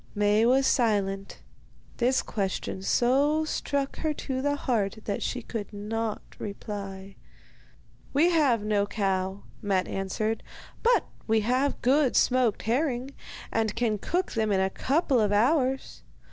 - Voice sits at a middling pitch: No, high, 225 Hz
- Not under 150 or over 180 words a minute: No, slow, 135 wpm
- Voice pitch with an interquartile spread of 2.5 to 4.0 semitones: No, average, 4.6 semitones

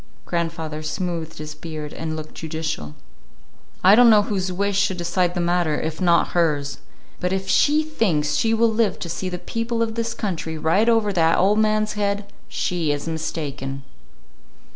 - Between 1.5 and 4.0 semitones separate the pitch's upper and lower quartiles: No, average, 4.7 semitones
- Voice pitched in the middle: Yes, medium, 175 Hz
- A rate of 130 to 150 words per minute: No, average, 170 wpm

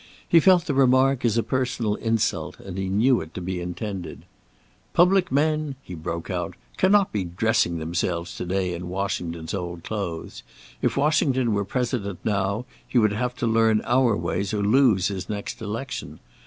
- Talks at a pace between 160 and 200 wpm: Yes, average, 170 wpm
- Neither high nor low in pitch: No, low, 105 Hz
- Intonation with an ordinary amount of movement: No, wide, 5.8 semitones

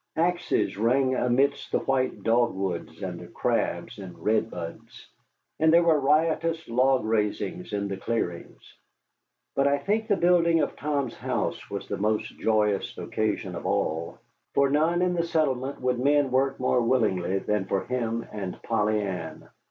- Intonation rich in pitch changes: Yes, wide, 6.0 semitones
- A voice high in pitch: No, low, 125 Hz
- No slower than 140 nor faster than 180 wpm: Yes, average, 160 wpm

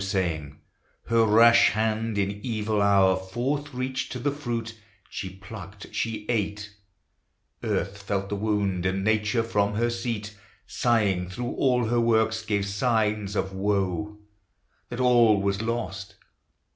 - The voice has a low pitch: Yes, low, 105 Hz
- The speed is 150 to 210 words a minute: No, average, 140 wpm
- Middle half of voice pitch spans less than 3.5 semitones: Yes, average, 2.8 semitones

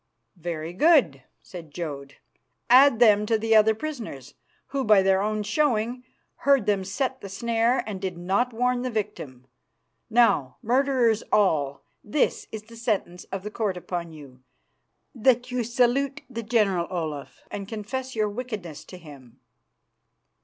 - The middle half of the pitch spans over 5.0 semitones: Yes, wide, 5.6 semitones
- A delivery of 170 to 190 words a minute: No, average, 145 wpm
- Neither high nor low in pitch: No, high, 215 Hz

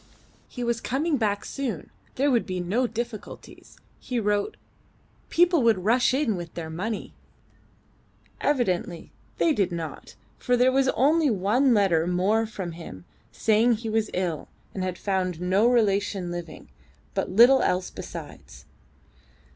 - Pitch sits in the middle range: No, high, 215 Hz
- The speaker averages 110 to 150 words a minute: Yes, average, 140 wpm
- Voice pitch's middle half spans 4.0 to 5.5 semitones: Yes, average, 5.2 semitones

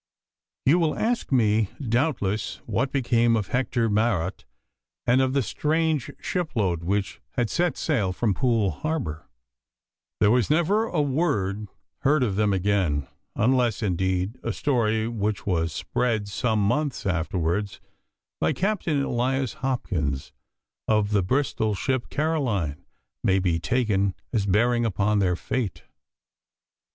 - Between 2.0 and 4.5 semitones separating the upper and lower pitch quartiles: No, average, 5.2 semitones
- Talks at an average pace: No, slow, 130 wpm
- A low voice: Yes, low, 110 Hz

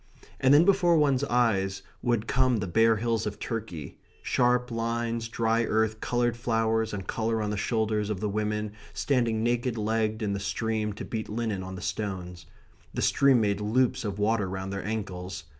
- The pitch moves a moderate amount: No, narrow, 2.2 semitones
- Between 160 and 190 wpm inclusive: Yes, average, 180 wpm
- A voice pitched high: No, low, 110 Hz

